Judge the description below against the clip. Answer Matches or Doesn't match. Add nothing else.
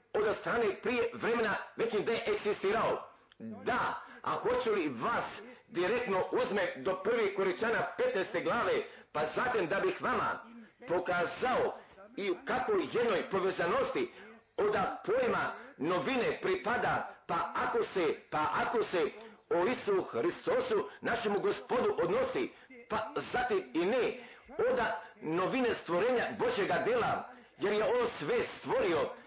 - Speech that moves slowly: Doesn't match